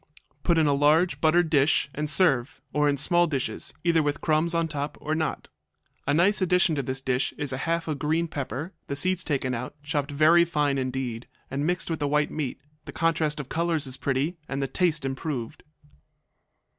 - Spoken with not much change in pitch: No, average, 3.2 semitones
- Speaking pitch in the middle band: Yes, medium, 150 Hz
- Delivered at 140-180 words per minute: No, average, 195 wpm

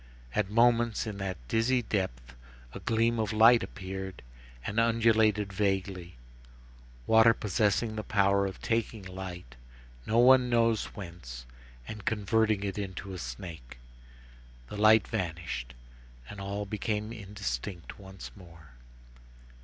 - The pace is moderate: No, slow, 120 wpm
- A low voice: Yes, low, 100 Hz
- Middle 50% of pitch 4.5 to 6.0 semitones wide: No, average, 3.2 semitones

